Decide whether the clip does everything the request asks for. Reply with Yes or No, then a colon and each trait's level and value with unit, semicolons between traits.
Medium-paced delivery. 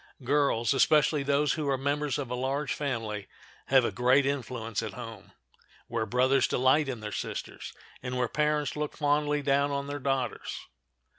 Yes: average, 165 wpm